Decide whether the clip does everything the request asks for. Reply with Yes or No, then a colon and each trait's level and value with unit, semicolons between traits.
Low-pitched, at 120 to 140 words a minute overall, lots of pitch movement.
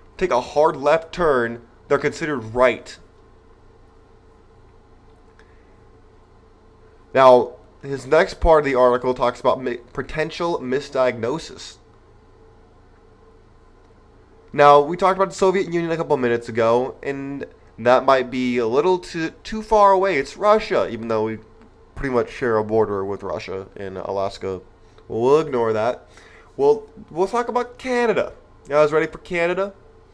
Yes: low, 120 Hz; slow, 135 wpm; wide, 7.9 semitones